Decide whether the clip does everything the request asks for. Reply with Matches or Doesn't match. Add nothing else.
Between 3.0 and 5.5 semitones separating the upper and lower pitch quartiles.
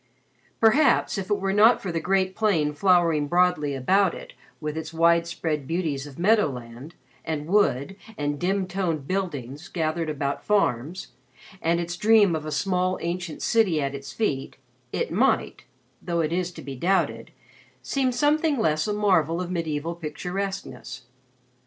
Matches